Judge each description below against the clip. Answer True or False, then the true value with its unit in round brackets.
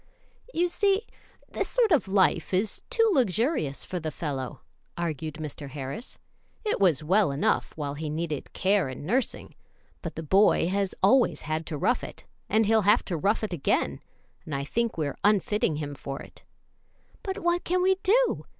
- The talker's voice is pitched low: False (190 Hz)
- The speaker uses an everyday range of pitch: False (7.8 semitones)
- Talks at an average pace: True (175 wpm)